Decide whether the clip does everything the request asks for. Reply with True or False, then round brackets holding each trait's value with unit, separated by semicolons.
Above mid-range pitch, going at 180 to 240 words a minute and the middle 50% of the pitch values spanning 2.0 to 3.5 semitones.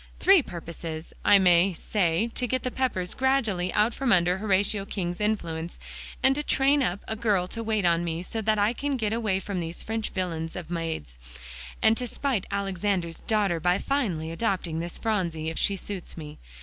False (195 Hz; 190 wpm; 4.6 semitones)